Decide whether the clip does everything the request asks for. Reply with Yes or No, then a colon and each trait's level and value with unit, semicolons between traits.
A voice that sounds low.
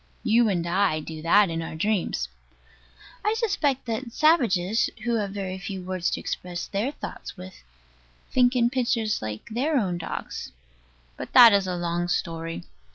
No: high, 195 Hz